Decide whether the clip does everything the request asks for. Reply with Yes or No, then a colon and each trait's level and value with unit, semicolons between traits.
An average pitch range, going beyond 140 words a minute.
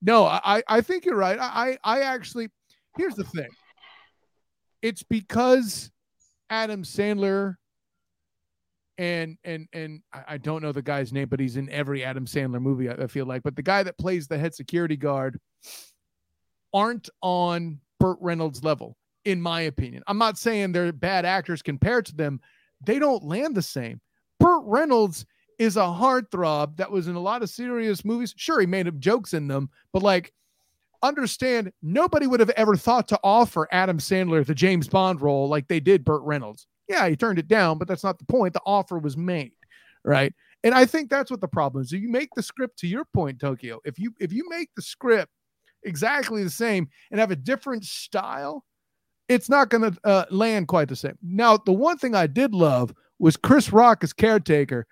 No: wide, 6.8 semitones; average, 190 wpm